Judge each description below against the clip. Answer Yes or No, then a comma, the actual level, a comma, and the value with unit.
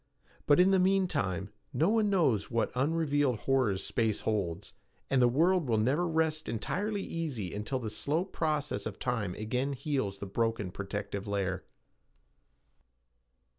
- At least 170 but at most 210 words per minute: No, average, 145 wpm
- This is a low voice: Yes, low, 130 Hz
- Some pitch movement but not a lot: No, wide, 7.4 semitones